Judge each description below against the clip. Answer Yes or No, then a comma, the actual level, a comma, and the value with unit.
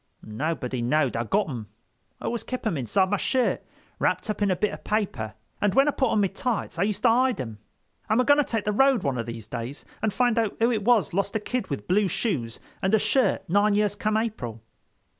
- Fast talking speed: Yes, fast, 235 wpm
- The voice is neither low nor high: No, high, 205 Hz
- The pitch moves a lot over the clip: Yes, wide, 8.3 semitones